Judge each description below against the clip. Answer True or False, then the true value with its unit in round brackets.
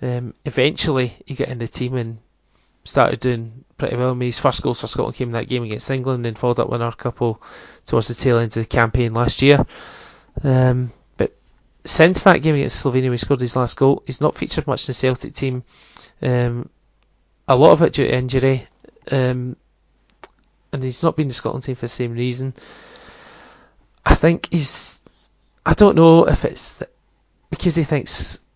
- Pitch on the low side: True (125 Hz)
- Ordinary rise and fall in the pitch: False (2.3 semitones)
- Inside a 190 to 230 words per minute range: True (195 wpm)